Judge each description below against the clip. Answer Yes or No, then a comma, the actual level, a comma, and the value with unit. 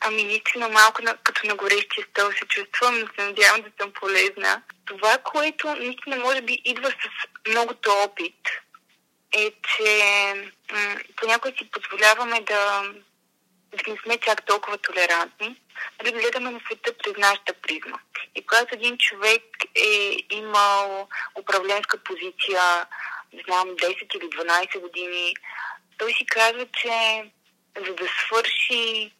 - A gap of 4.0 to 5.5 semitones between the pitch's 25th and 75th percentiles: No, average, 3.2 semitones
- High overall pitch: Yes, high, 215 Hz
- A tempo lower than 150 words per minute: Yes, average, 135 wpm